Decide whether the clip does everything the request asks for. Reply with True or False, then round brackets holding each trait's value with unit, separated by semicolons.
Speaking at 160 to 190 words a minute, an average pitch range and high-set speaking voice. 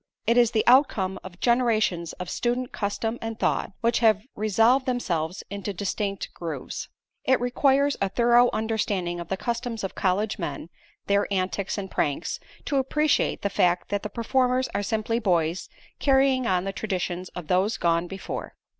True (165 wpm; 4.5 semitones; 210 Hz)